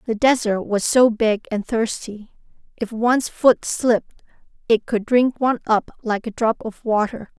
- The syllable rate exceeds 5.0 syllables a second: No, 4.5 syllables/s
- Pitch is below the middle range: No, high, 225 Hz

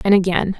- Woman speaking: Yes, female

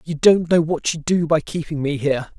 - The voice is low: No, medium, 160 Hz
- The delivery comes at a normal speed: No, fast, 250 wpm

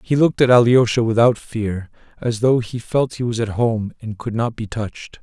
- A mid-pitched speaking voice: No, low, 115 Hz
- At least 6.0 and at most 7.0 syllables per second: No, 5.0 syllables/s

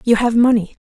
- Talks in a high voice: Yes, high, 230 Hz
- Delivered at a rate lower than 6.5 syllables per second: No, 6.6 syllables/s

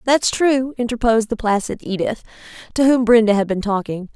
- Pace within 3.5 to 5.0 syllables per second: No, 5.8 syllables/s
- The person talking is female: Yes, female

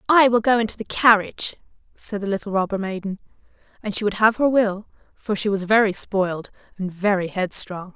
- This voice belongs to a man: No, female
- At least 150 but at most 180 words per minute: No, average, 190 wpm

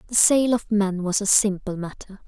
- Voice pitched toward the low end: No, high, 205 Hz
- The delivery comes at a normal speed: No, fast, 210 wpm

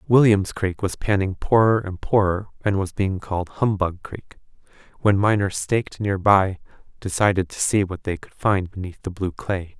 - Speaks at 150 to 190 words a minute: Yes, average, 180 wpm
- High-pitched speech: No, very low, 95 Hz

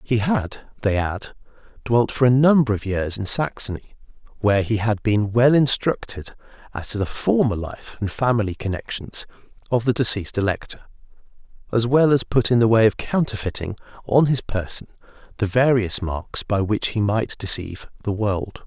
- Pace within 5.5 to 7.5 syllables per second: No, 5.0 syllables/s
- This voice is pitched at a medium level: No, low, 110 Hz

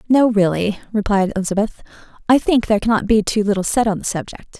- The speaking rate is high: No, average, 195 wpm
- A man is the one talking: No, female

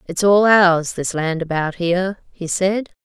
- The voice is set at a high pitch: No, medium, 180 Hz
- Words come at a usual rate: Yes, average, 180 wpm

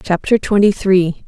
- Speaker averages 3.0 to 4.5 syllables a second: Yes, 4.3 syllables/s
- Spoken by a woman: Yes, female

